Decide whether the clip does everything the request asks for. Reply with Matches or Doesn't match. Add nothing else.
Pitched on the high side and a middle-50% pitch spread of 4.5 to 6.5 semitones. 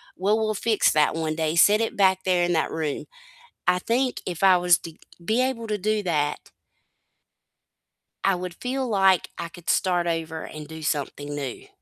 Doesn't match